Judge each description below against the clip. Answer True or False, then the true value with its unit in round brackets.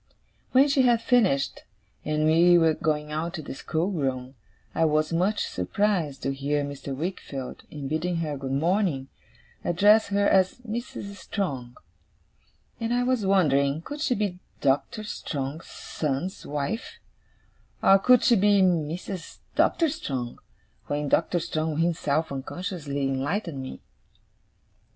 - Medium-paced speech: False (130 wpm)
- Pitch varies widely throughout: True (6.1 semitones)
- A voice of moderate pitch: True (165 Hz)